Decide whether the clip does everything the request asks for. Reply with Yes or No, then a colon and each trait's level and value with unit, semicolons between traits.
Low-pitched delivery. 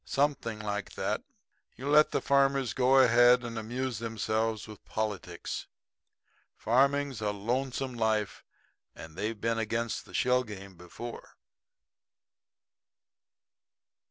Yes: low, 115 Hz